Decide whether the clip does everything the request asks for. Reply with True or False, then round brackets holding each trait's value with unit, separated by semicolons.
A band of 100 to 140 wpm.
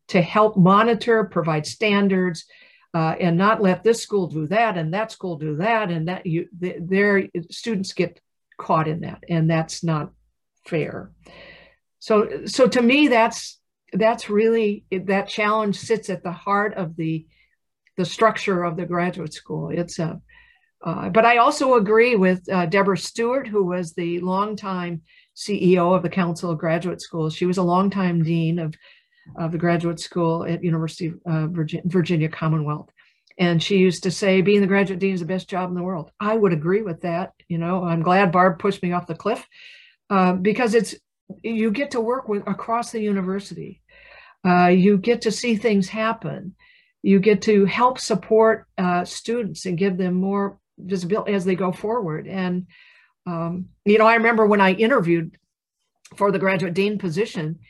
False (175 wpm)